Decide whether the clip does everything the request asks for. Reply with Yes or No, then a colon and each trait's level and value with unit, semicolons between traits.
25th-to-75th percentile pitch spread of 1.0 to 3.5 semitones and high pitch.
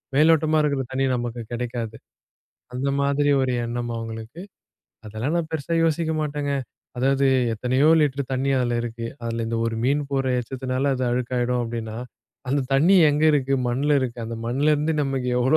No: average, 3.2 semitones; low, 130 Hz